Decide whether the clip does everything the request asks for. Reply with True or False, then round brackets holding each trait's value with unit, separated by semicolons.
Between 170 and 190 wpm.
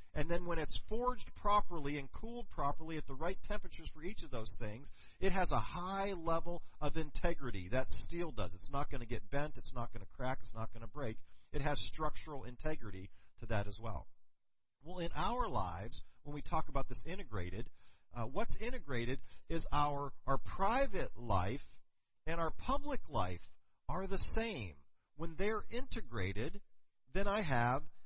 True (180 wpm)